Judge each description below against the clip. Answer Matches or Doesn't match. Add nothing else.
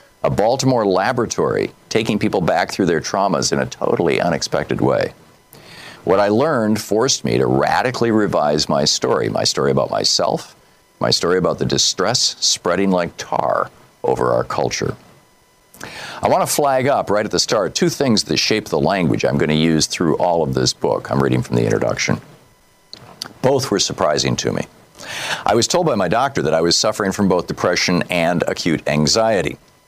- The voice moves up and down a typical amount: Doesn't match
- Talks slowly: Doesn't match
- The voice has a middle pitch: Doesn't match